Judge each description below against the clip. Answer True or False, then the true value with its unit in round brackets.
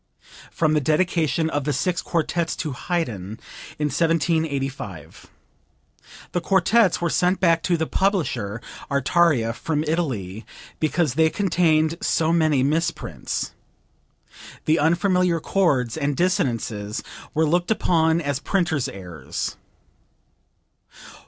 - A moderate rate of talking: False (110 wpm)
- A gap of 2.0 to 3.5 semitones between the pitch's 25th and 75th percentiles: False (4.1 semitones)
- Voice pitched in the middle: True (160 Hz)